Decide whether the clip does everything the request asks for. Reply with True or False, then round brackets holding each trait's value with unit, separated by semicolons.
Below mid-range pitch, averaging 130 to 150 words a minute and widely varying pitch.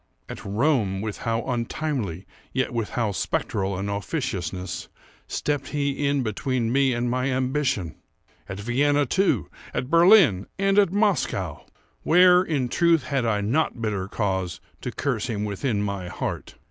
True (120 Hz; 140 wpm; 6.2 semitones)